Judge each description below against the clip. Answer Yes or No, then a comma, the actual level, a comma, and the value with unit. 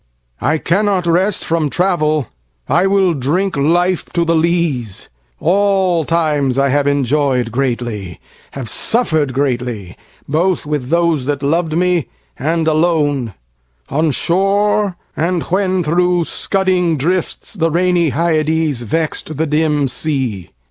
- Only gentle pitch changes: No, average, 4.0 semitones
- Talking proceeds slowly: Yes, slow, 110 wpm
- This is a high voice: No, medium, 160 Hz